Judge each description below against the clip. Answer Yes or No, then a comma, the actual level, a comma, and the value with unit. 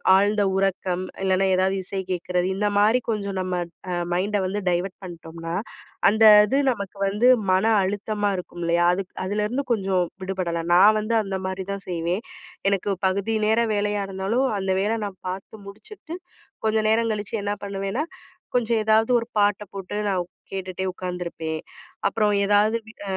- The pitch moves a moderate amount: No, narrow, 2.3 semitones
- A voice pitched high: Yes, high, 195 Hz